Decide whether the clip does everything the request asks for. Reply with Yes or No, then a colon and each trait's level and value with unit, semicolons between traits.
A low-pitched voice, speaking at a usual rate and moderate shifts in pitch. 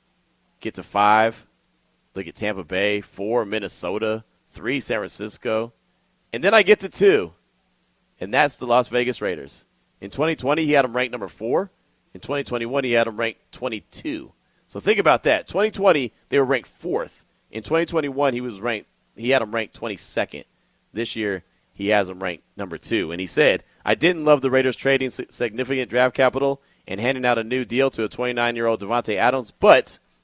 Yes: low, 120 Hz; average, 180 wpm; average, 4.0 semitones